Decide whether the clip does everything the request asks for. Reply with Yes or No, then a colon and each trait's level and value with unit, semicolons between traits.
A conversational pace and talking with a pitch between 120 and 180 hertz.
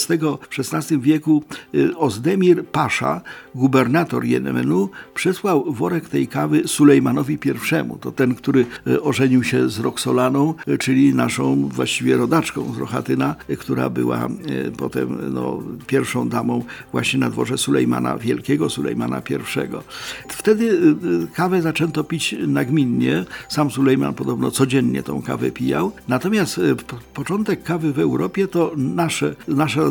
Yes: average, 120 wpm; low, 130 Hz